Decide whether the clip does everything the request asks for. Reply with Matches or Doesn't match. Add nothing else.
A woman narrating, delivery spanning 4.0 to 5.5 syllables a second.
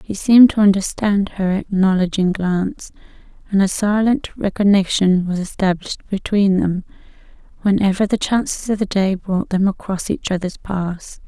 Matches